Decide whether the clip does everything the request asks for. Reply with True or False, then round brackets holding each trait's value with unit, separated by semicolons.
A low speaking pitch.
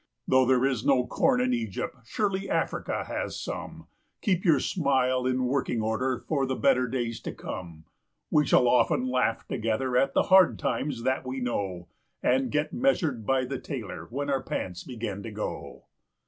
True (130 Hz)